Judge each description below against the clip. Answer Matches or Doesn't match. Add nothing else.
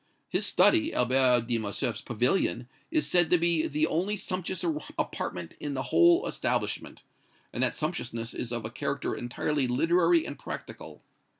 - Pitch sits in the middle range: Matches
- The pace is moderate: Matches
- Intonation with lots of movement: Matches